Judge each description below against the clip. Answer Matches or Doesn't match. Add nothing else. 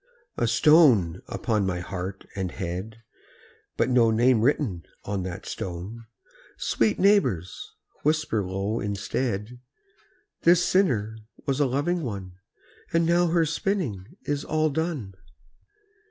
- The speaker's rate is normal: Doesn't match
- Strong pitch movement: Matches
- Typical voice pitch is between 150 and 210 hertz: Doesn't match